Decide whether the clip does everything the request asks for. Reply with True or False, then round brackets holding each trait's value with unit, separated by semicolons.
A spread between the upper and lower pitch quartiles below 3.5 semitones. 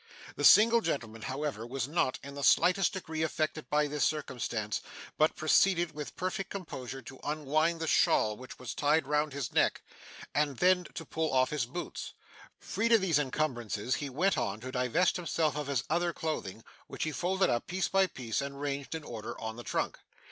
False (4.6 semitones)